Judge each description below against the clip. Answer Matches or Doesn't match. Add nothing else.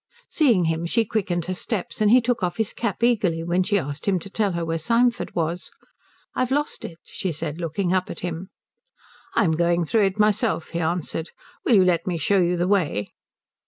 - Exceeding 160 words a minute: Matches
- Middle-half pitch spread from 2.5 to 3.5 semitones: Doesn't match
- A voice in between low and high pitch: Matches